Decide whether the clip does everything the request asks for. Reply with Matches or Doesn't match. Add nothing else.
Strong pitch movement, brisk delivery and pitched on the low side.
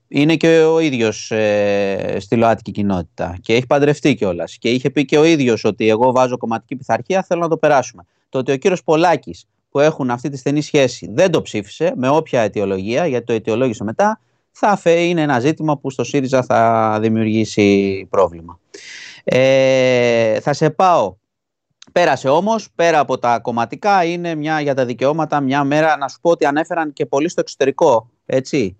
Matches